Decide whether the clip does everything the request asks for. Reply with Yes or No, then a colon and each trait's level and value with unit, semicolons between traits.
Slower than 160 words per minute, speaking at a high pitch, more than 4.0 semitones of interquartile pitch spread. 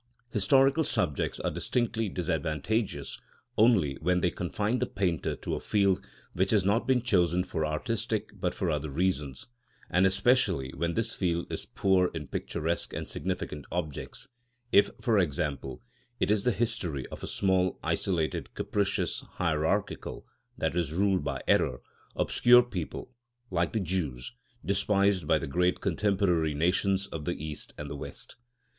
No: average, 145 wpm; very low, 90 Hz; average, 4.7 semitones